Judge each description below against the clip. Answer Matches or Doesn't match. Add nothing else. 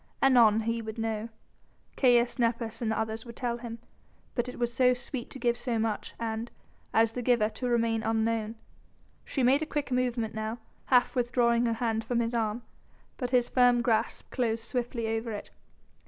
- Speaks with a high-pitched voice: Matches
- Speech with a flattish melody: Matches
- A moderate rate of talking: Matches